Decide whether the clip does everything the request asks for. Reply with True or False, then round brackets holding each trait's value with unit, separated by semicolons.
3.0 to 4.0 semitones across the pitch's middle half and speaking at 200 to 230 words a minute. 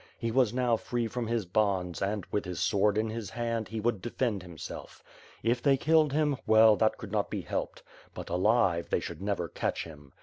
True (3.5 semitones; 205 wpm)